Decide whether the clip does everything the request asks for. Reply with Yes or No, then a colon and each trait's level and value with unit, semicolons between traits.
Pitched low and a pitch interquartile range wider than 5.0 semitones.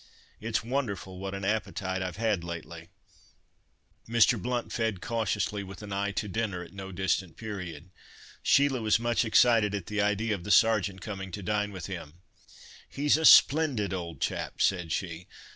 No: low, 100 Hz; average, 3.1 semitones